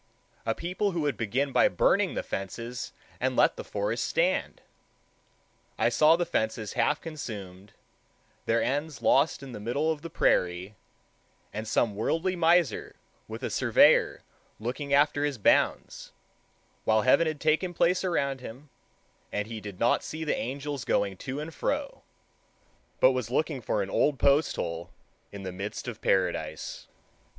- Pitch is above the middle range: No, low, 135 Hz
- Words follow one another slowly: No, average, 155 wpm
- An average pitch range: No, wide, 6.8 semitones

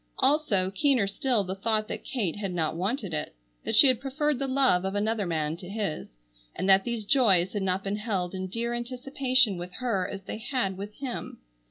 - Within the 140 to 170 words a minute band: No, fast, 205 wpm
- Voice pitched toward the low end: No, high, 210 Hz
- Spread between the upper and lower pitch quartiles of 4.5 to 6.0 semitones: Yes, average, 5.0 semitones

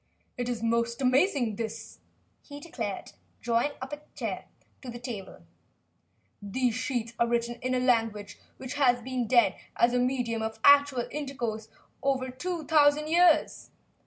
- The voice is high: Yes, very high, 250 Hz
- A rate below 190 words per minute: Yes, average, 155 wpm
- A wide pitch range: No, average, 3.0 semitones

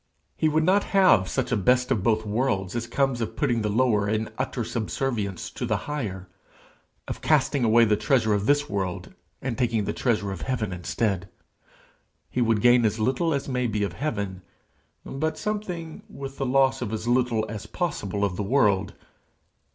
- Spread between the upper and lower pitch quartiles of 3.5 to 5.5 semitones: Yes, average, 4.4 semitones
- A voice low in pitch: Yes, low, 120 Hz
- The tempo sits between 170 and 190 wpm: Yes, average, 180 wpm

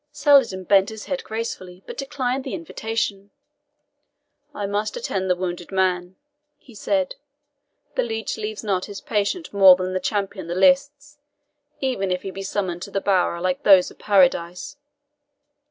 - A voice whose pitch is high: Yes, high, 200 Hz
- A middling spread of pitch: Yes, average, 3.5 semitones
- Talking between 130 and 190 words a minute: Yes, average, 155 wpm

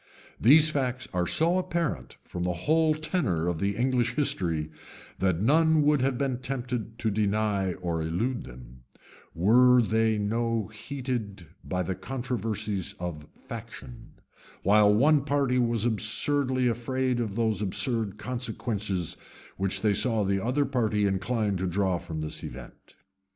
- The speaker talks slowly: No, average, 145 wpm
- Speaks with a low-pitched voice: Yes, low, 110 Hz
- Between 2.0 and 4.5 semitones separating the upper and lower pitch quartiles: No, average, 5.0 semitones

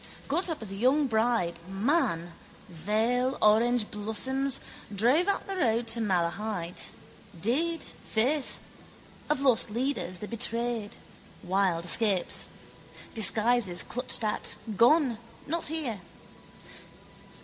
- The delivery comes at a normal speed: No, slow, 105 wpm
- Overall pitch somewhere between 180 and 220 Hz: No, high, 230 Hz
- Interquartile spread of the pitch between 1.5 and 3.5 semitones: No, average, 4.6 semitones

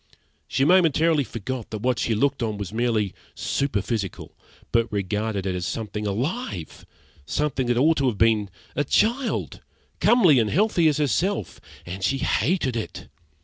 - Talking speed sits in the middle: Yes, average, 150 wpm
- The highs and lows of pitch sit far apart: Yes, wide, 6.1 semitones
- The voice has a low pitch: Yes, low, 120 Hz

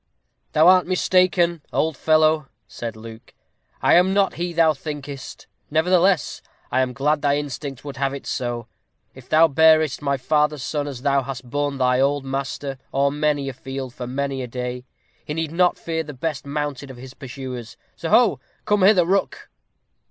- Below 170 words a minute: No, average, 175 wpm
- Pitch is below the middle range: No, medium, 145 Hz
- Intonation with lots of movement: No, average, 3.3 semitones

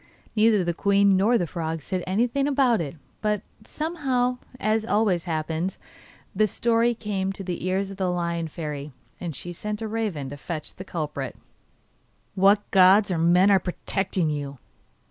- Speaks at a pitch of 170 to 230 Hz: Yes, high, 190 Hz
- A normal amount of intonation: Yes, average, 4.2 semitones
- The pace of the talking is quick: No, average, 165 wpm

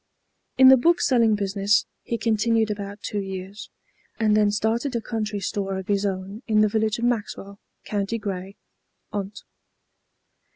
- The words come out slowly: No, average, 150 wpm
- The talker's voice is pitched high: Yes, high, 210 Hz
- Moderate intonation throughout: No, narrow, 2.1 semitones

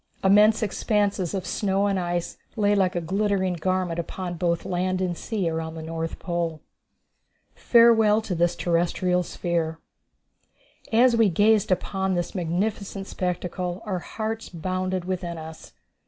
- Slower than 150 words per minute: Yes, average, 140 wpm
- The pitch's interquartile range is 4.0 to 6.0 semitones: No, average, 2.8 semitones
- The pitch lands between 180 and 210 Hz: Yes, medium, 185 Hz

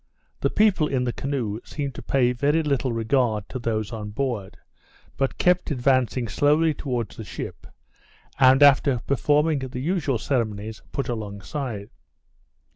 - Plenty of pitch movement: No, average, 4.0 semitones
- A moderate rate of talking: Yes, average, 145 wpm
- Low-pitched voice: Yes, low, 130 Hz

